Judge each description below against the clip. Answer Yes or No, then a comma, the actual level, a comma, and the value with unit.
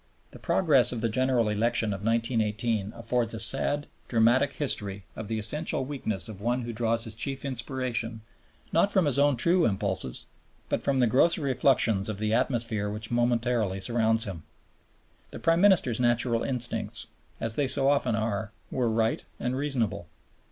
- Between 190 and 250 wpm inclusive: No, average, 165 wpm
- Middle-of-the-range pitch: No, low, 115 Hz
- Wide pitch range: No, average, 3.2 semitones